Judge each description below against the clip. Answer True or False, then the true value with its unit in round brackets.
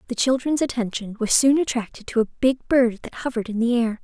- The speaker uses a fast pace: True (225 wpm)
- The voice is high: True (240 Hz)